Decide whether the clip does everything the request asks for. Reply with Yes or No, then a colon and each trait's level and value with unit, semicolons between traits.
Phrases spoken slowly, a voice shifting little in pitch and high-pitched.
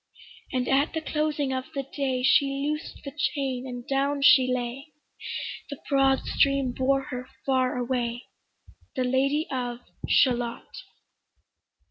Yes: slow, 130 wpm; narrow, 1.7 semitones; very high, 270 Hz